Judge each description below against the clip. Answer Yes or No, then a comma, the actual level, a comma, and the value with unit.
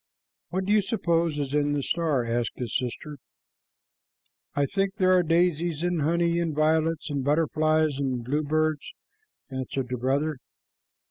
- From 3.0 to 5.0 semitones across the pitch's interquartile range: Yes, average, 3.3 semitones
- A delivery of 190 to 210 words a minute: No, average, 145 wpm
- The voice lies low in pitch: No, medium, 155 Hz